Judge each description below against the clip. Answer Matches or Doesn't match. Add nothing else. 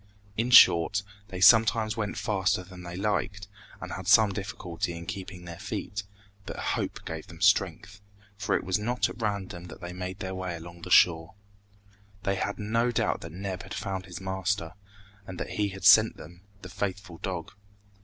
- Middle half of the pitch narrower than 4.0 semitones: Matches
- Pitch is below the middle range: Matches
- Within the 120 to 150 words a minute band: Doesn't match